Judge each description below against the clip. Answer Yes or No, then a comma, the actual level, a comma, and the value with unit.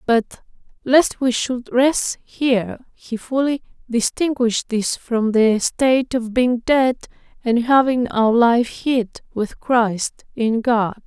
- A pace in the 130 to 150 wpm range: Yes, slow, 135 wpm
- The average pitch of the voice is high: Yes, high, 240 Hz